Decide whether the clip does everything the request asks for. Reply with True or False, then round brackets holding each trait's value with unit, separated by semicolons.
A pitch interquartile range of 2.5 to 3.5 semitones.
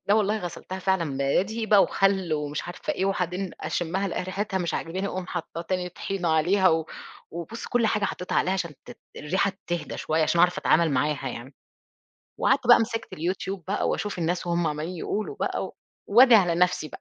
True (2.9 semitones)